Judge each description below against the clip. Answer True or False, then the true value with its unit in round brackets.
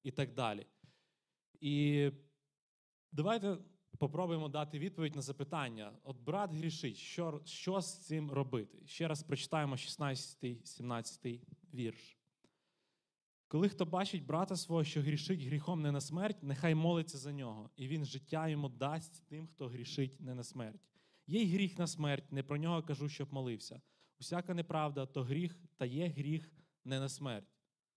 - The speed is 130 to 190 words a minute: True (150 wpm)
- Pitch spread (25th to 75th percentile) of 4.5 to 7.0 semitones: False (3.6 semitones)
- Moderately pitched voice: True (150 Hz)